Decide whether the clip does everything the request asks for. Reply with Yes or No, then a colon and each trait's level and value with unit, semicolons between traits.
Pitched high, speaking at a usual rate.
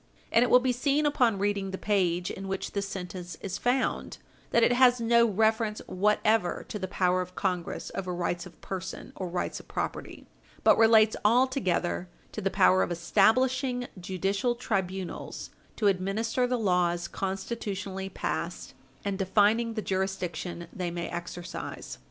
Yes: high, 195 Hz; average, 155 wpm